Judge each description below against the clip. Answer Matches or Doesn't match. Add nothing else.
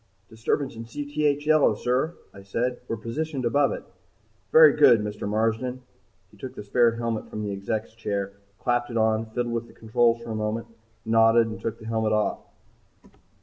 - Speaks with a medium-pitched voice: Doesn't match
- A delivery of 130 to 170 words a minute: Doesn't match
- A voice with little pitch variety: Matches